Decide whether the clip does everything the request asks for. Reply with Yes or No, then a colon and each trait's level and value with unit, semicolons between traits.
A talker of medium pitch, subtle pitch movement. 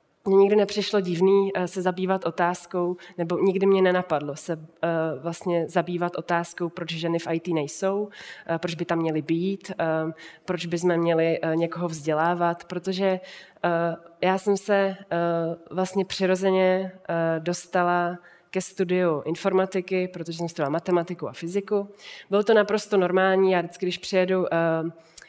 Yes: medium, 175 Hz; narrow, 2.1 semitones